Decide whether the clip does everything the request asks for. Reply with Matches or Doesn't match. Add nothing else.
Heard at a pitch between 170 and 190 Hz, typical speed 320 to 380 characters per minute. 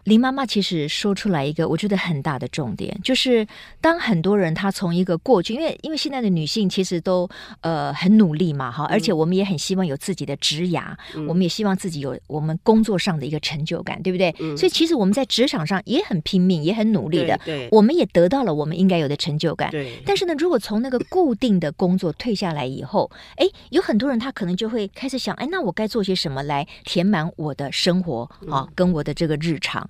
Matches